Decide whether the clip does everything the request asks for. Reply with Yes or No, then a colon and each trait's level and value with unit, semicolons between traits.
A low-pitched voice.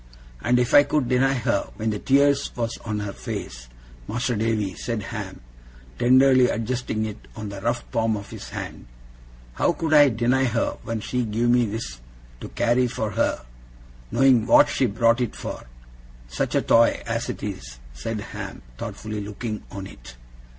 Yes: low, 115 Hz